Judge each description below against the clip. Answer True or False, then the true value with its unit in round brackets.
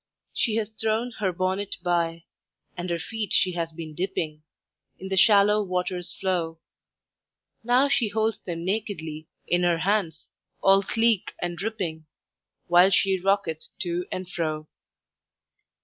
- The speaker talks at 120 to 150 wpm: True (135 wpm)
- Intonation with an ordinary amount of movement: True (3.5 semitones)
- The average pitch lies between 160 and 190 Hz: True (185 Hz)